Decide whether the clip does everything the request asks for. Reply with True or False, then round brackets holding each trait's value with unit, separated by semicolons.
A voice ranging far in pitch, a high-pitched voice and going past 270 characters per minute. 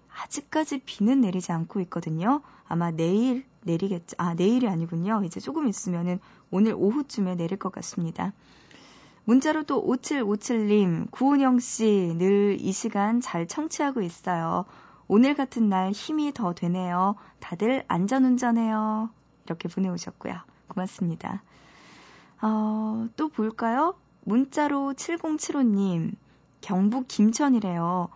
False (5.7 semitones; 210 Hz; 260 characters per minute)